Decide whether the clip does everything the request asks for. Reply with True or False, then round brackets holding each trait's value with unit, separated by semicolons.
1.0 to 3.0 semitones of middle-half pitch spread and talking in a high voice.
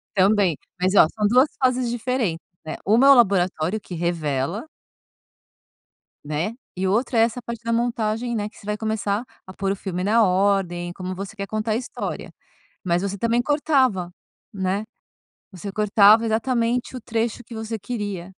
False (3.8 semitones; 210 Hz)